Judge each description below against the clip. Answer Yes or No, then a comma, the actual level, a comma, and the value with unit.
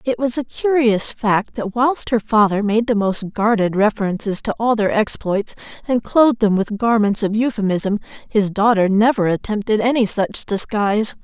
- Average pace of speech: Yes, average, 170 wpm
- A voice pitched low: No, high, 215 Hz